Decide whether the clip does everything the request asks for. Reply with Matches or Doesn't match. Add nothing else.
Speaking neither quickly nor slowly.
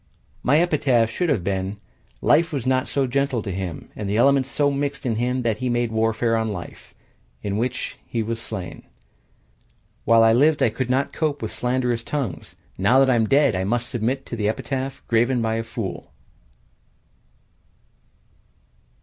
Matches